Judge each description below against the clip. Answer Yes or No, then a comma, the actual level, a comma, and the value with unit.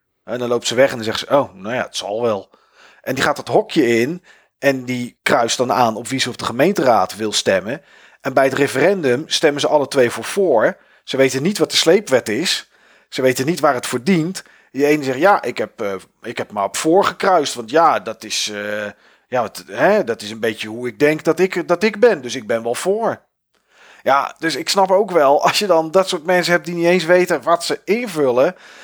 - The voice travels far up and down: Yes, wide, 6.3 semitones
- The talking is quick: Yes, fast, 240 wpm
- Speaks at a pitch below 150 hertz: Yes, medium, 140 Hz